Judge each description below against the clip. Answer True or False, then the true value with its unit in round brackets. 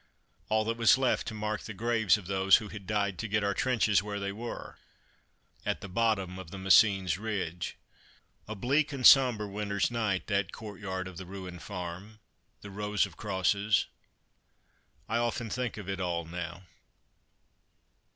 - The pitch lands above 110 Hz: False (100 Hz)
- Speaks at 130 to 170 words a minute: True (165 wpm)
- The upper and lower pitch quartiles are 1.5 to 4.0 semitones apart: True (2.8 semitones)